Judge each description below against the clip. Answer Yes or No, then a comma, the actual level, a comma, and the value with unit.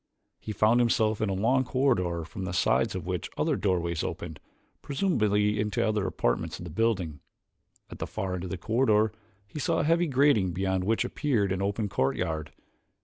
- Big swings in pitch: No, average, 4.0 semitones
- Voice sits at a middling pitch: No, low, 100 Hz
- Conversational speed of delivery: Yes, average, 185 wpm